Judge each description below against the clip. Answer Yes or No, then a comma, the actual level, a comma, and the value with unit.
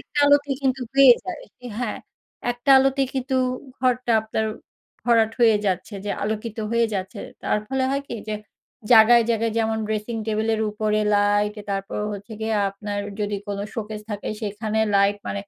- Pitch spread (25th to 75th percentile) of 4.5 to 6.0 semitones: No, average, 2.8 semitones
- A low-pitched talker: No, high, 220 Hz